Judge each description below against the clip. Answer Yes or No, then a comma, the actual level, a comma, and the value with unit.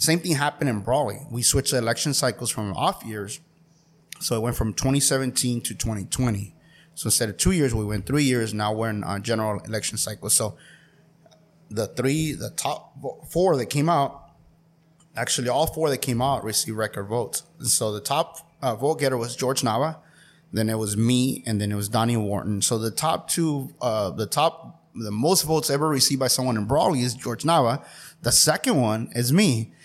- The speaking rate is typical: Yes, average, 195 wpm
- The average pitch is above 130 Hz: No, low, 125 Hz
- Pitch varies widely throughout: Yes, wide, 5.9 semitones